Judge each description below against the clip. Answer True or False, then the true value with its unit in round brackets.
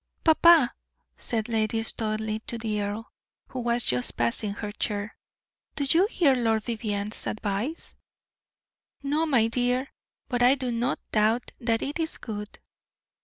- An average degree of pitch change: True (3.2 semitones)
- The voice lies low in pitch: False (230 Hz)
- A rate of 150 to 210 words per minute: False (140 wpm)